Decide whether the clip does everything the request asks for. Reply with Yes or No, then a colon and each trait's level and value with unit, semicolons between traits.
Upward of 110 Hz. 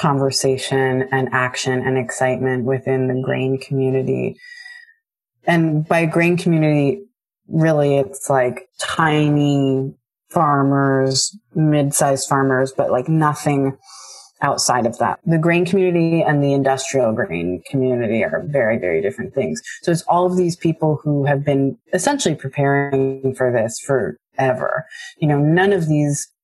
Yes: medium, 140 Hz